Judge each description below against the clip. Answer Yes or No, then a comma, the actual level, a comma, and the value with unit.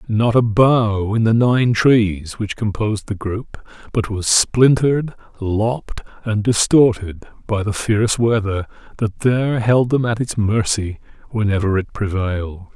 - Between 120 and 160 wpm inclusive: Yes, average, 145 wpm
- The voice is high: No, low, 110 Hz